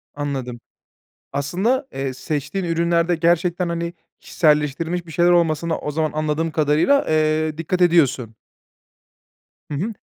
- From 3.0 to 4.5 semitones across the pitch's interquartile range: No, narrow, 2.6 semitones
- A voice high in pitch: No, medium, 160 Hz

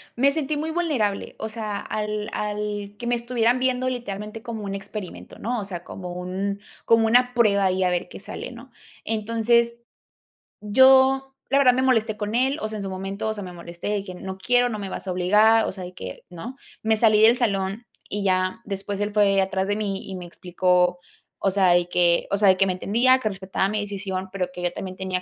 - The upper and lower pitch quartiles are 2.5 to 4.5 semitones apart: Yes, average, 3.5 semitones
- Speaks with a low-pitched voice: No, high, 205 Hz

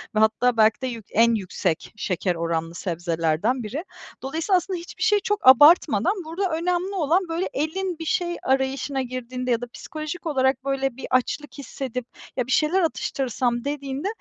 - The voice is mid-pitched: No, very high, 265 Hz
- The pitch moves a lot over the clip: Yes, wide, 5.8 semitones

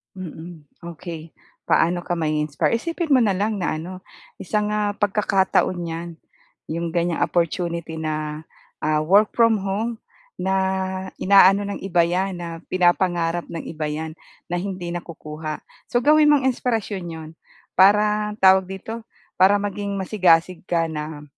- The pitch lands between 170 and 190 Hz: Yes, medium, 185 Hz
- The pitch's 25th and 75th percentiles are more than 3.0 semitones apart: Yes, average, 3.6 semitones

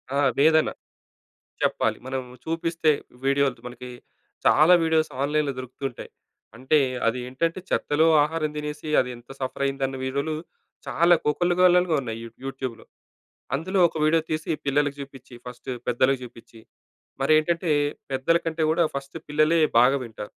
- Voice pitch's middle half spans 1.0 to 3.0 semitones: No, average, 3.5 semitones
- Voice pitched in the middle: Yes, medium, 145 Hz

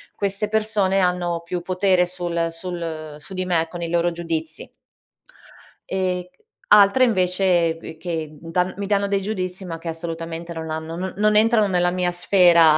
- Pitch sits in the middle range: Yes, medium, 180 Hz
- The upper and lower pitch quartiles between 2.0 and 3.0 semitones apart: Yes, narrow, 2.4 semitones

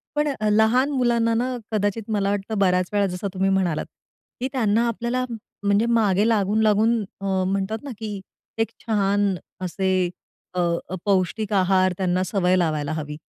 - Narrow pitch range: No, average, 3.0 semitones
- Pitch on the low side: No, high, 200 Hz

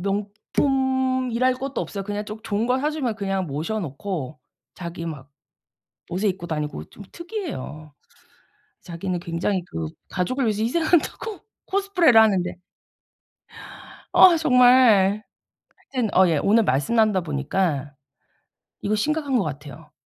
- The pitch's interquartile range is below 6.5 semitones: No, wide, 7.3 semitones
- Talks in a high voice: Yes, high, 205 Hz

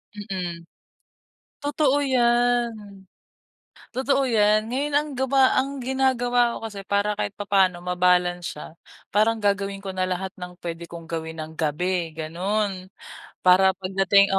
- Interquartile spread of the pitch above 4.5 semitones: Yes, average, 5.1 semitones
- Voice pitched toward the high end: Yes, high, 200 Hz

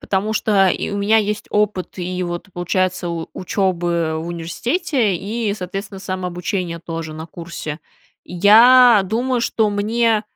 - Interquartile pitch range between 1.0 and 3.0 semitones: No, average, 3.7 semitones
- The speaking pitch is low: No, high, 190 Hz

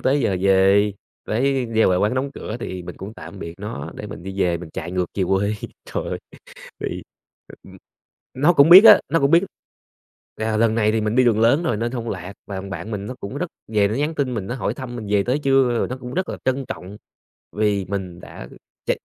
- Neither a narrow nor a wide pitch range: Yes, average, 5.0 semitones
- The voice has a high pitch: No, low, 110 Hz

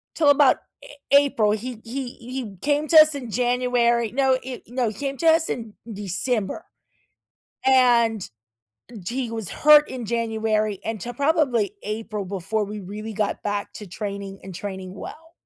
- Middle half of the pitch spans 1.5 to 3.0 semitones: No, average, 4.1 semitones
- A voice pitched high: Yes, high, 230 Hz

